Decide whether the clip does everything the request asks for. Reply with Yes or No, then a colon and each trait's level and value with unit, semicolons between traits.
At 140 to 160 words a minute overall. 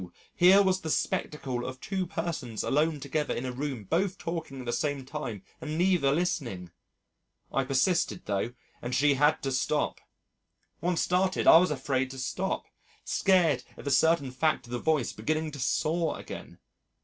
No: average, 170 wpm